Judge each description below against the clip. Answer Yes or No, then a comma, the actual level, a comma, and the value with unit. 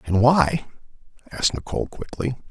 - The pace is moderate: No, slow, 120 wpm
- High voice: No, low, 105 Hz